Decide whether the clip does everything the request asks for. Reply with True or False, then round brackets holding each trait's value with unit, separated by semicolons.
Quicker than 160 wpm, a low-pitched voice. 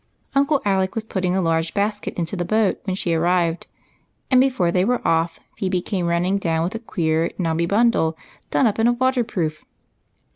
False (190 wpm; 185 Hz)